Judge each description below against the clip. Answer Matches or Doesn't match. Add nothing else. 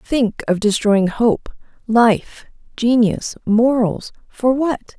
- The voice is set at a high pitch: Matches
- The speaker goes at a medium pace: Doesn't match